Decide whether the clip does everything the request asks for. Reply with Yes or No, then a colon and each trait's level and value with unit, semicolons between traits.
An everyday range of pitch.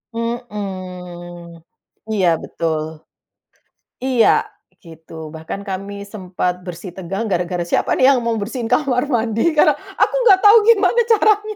No: wide, 5.8 semitones